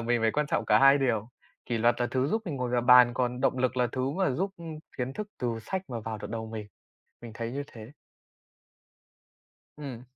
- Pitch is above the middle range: No, low, 125 Hz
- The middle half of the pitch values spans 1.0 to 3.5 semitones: Yes, average, 2.9 semitones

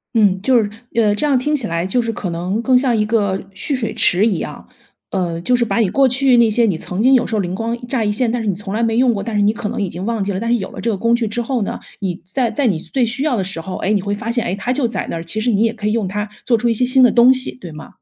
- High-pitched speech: Yes, high, 225 Hz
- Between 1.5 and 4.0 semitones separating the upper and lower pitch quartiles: Yes, average, 3.7 semitones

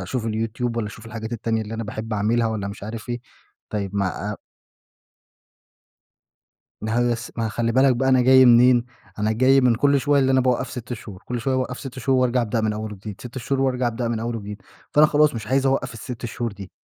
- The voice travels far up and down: No, average, 2.7 semitones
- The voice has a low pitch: Yes, low, 115 Hz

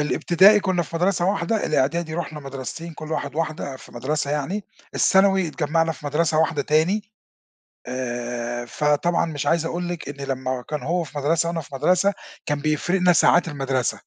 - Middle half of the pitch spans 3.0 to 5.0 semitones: Yes, average, 3.6 semitones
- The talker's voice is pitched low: No, medium, 155 Hz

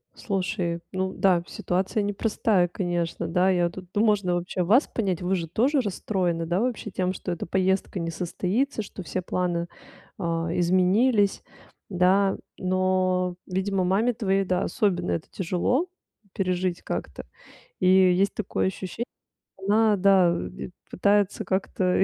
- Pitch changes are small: Yes, narrow, 2.1 semitones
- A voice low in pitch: No, medium, 185 Hz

